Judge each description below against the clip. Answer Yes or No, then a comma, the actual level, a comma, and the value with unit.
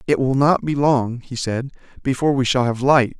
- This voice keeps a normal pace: No, fast, 225 wpm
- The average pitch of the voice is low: Yes, low, 130 Hz